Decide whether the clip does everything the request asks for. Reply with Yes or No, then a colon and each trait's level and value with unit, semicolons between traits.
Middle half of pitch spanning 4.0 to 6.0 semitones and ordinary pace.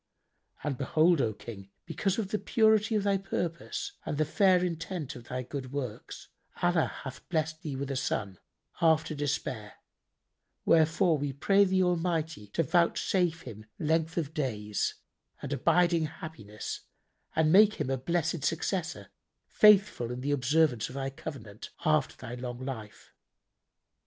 Yes: average, 5.2 semitones; average, 145 wpm